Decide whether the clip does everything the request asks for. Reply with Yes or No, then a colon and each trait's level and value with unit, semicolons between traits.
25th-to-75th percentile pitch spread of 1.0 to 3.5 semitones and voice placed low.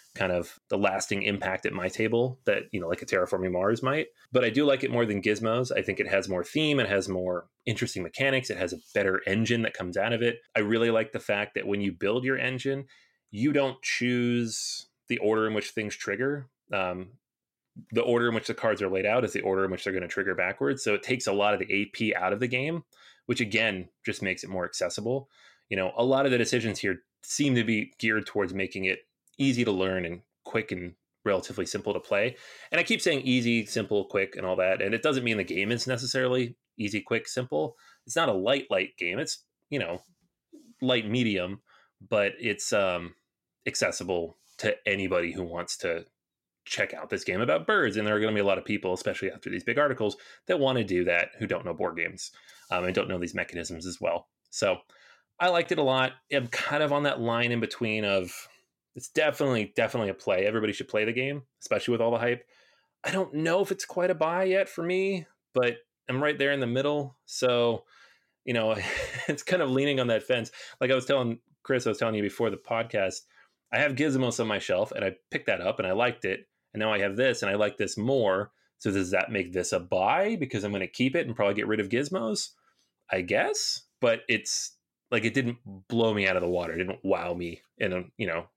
No: average, 5.1 semitones; low, 115 Hz